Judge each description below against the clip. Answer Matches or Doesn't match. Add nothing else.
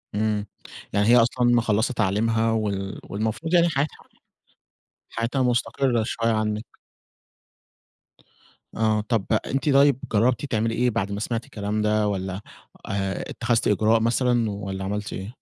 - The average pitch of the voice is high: Doesn't match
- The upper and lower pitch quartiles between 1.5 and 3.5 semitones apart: Matches